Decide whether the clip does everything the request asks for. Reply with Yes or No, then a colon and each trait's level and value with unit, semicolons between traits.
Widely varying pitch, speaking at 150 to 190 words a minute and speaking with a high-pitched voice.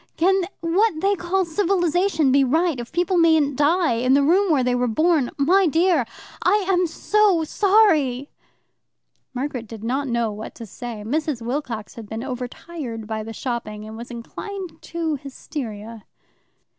Yes: wide, 6.7 semitones; average, 160 wpm; very high, 285 Hz